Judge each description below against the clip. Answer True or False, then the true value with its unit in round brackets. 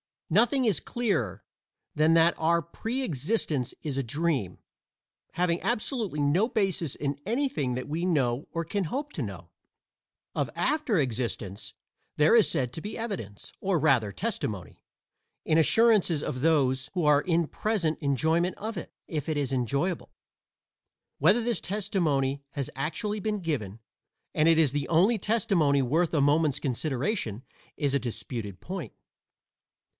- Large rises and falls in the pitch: True (6.4 semitones)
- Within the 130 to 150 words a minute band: True (145 wpm)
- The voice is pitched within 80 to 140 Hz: False (160 Hz)